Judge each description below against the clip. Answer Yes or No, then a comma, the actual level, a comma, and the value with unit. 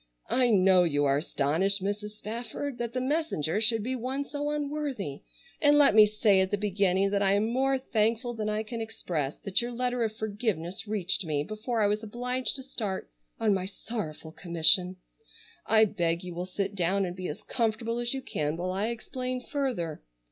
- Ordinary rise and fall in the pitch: Yes, average, 4.6 semitones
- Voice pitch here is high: Yes, high, 210 Hz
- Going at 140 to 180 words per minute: No, average, 190 wpm